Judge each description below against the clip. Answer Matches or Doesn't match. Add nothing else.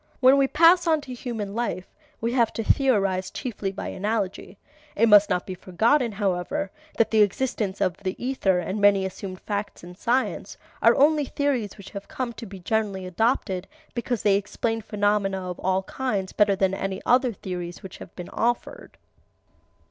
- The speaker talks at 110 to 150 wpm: Doesn't match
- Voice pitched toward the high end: Matches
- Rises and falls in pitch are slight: Doesn't match